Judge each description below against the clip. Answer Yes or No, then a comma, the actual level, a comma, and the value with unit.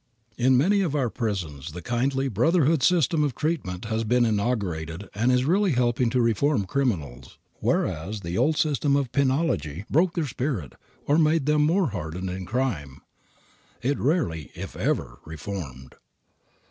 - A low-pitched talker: Yes, low, 125 Hz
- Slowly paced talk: No, average, 160 wpm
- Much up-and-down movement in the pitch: Yes, wide, 8.0 semitones